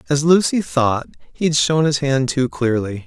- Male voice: Yes, male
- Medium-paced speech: Yes, average, 195 wpm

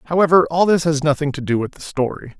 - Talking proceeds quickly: Yes, fast, 250 wpm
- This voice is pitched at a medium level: Yes, medium, 155 Hz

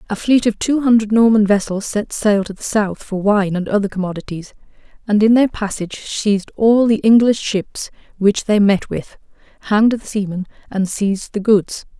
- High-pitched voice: Yes, high, 210 Hz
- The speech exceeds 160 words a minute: Yes, average, 185 wpm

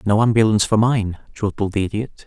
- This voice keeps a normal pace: Yes, average, 185 wpm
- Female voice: No, male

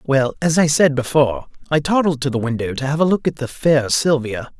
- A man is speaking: Yes, male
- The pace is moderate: No, fast, 235 wpm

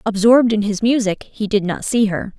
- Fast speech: Yes, fast, 225 wpm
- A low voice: No, high, 215 Hz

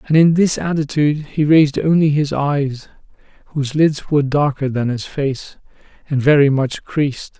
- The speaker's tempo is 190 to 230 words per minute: No, average, 160 wpm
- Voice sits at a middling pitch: Yes, medium, 145 Hz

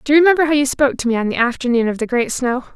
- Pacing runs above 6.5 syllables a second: Yes, 7.7 syllables/s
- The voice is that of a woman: Yes, female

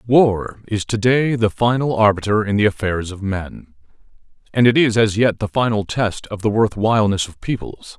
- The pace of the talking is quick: No, average, 195 wpm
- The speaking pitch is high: No, low, 105 Hz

